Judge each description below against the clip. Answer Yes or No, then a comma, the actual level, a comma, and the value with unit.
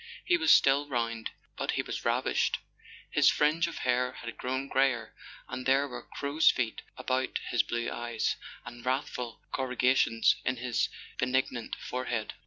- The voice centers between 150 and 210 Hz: No, low, 125 Hz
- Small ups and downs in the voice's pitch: Yes, narrow, 2.2 semitones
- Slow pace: No, average, 150 wpm